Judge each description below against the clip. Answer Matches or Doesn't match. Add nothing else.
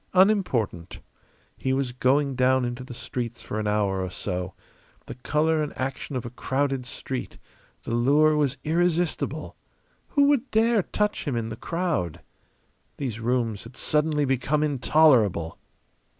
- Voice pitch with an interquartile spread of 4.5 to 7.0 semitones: Matches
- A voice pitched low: Matches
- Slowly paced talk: Doesn't match